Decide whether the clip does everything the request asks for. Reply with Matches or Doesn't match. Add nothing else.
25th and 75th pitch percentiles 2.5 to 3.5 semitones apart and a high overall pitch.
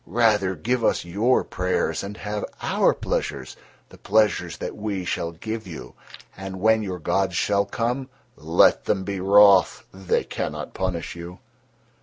Doesn't match